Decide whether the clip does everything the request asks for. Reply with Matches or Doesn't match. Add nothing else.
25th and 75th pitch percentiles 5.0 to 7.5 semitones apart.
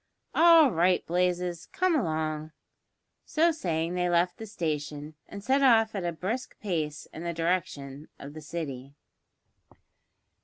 Matches